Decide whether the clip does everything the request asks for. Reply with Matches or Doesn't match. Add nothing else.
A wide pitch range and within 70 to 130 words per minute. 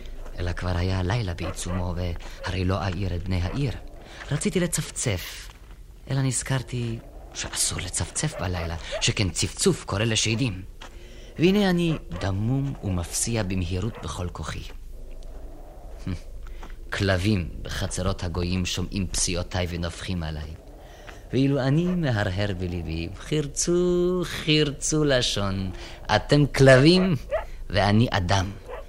Matches